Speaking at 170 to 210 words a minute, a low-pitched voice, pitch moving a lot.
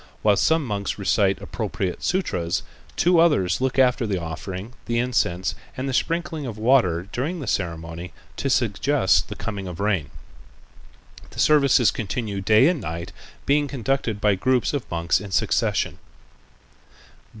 No: average, 145 wpm; low, 110 Hz; wide, 6.6 semitones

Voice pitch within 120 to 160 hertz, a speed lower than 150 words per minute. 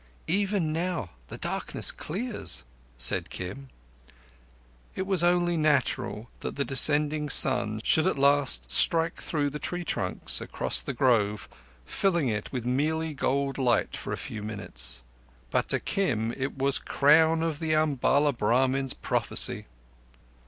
Yes: medium, 140 Hz; average, 140 wpm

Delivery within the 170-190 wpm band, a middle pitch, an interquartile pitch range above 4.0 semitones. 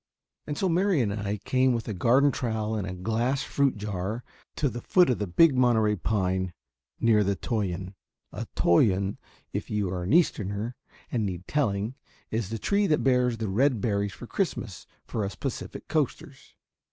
No: average, 175 wpm; low, 110 Hz; average, 4.4 semitones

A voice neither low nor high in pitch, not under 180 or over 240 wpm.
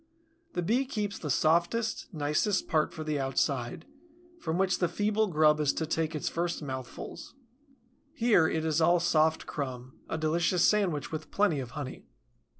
No: medium, 160 Hz; average, 160 wpm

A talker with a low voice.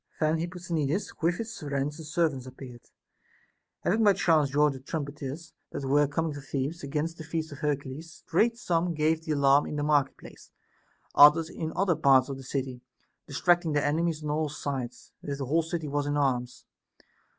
No: medium, 150 Hz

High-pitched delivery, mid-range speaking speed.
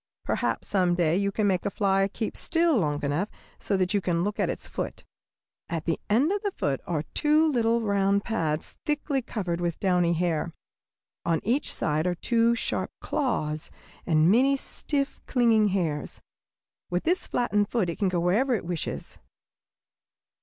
Yes: high, 195 Hz; average, 170 wpm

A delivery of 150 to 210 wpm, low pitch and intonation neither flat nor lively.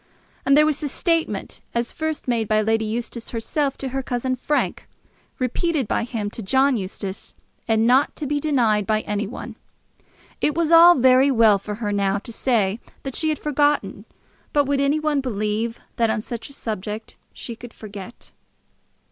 No: average, 180 wpm; high, 240 Hz; average, 4.7 semitones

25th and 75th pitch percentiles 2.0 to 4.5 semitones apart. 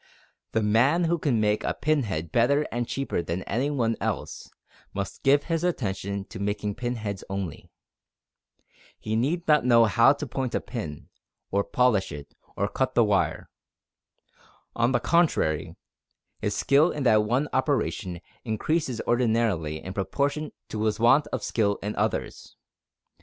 No: wide, 5.5 semitones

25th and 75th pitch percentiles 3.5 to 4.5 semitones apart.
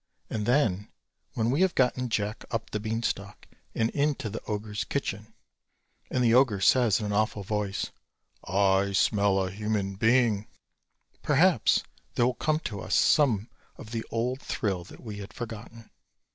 No: average, 3.0 semitones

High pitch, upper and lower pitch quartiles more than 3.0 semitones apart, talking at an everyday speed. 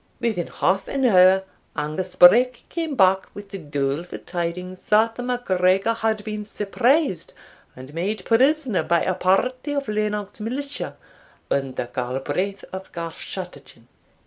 No: high, 195 Hz; average, 4.6 semitones; slow, 130 wpm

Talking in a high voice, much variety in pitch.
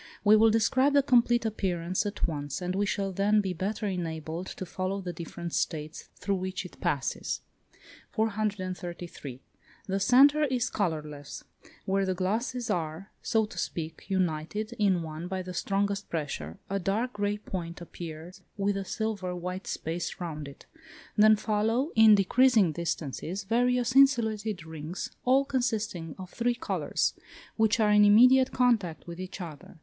No: high, 195 Hz; average, 4.2 semitones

